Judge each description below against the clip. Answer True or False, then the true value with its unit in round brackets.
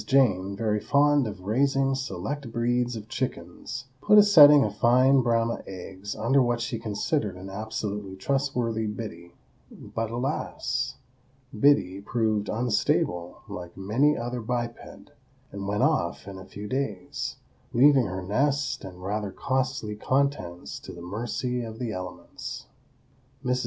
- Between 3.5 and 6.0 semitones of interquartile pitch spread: True (4.7 semitones)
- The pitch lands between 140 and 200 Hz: False (115 Hz)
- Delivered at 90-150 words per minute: True (135 wpm)